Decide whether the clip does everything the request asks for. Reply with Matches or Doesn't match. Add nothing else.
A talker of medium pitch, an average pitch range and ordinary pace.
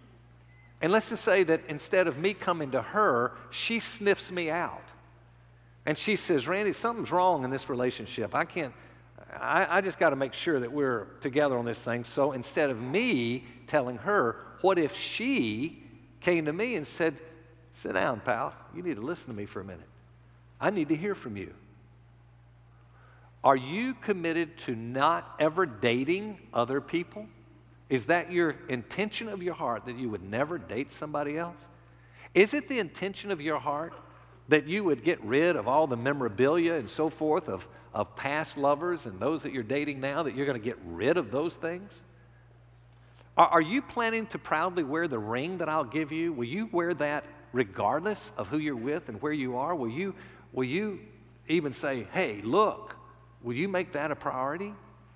Doesn't match